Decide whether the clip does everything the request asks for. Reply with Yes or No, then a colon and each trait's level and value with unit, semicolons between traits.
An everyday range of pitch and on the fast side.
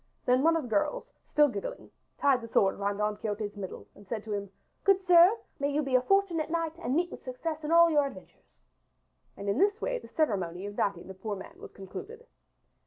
No: wide, 8.6 semitones; fast, 215 wpm